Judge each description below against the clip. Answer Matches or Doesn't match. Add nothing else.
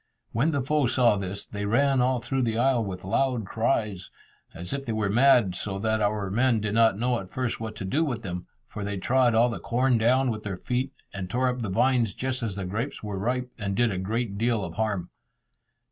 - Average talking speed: Doesn't match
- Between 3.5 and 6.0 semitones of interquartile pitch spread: Matches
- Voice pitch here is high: Doesn't match